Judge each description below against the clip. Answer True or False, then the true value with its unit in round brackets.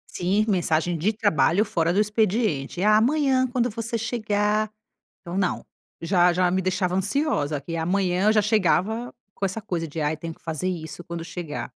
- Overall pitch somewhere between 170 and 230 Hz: True (190 Hz)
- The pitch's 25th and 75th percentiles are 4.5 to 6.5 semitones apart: False (4.1 semitones)